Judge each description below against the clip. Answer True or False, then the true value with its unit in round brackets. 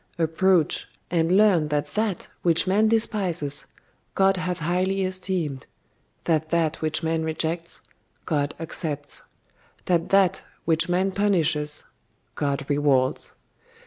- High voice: False (165 Hz)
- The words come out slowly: True (115 wpm)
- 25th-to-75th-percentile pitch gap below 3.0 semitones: False (3.6 semitones)